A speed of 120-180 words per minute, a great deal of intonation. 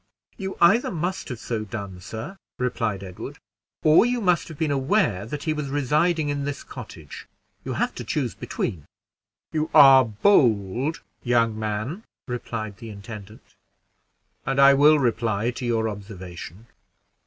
Yes: average, 145 wpm; wide, 6.0 semitones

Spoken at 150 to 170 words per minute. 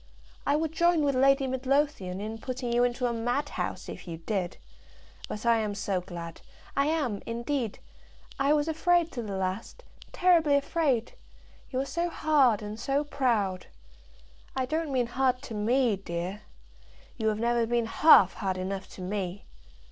Yes: average, 165 wpm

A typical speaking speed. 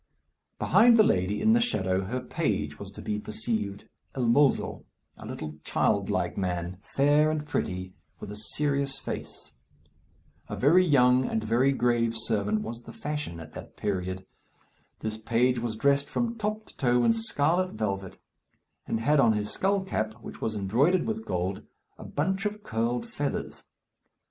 Yes: average, 165 wpm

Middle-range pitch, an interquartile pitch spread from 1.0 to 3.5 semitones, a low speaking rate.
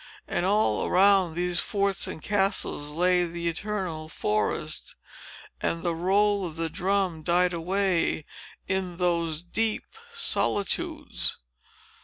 Yes: medium, 180 Hz; average, 2.9 semitones; slow, 115 wpm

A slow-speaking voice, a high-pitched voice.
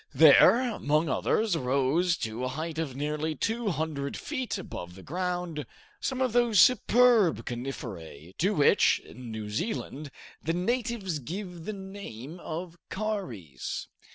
No: slow, 130 wpm; medium, 165 Hz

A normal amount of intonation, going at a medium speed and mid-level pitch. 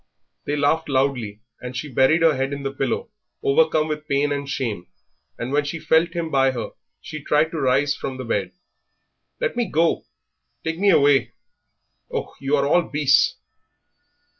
Yes: average, 3.1 semitones; average, 170 wpm; medium, 145 Hz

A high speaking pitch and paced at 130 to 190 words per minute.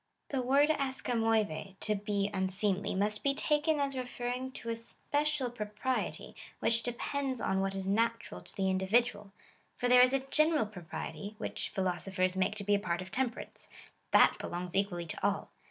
Yes: high, 220 Hz; average, 180 wpm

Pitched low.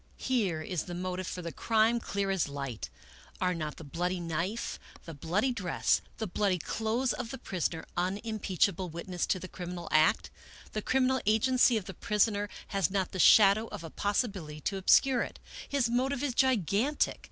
No: high, 195 Hz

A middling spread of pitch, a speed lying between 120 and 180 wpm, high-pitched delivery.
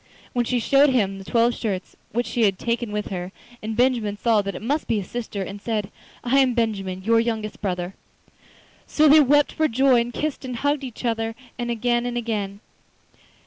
No: average, 3.1 semitones; average, 195 wpm; high, 230 Hz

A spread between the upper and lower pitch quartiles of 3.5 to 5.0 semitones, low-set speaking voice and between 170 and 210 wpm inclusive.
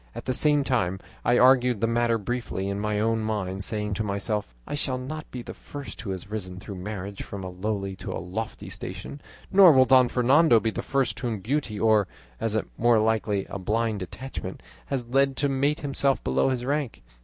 Yes: average, 4.5 semitones; low, 115 Hz; fast, 205 wpm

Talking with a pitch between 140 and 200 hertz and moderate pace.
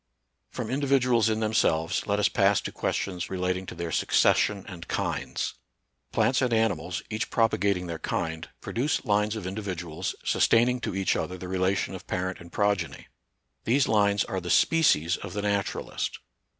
No: low, 100 Hz; average, 160 wpm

